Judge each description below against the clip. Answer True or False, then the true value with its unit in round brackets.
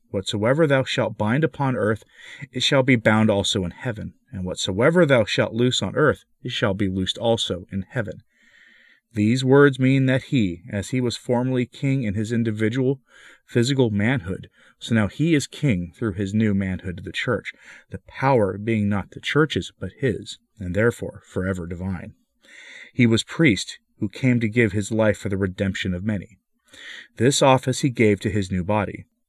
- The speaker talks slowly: False (180 wpm)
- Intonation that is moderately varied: True (4.6 semitones)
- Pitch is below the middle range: True (110 Hz)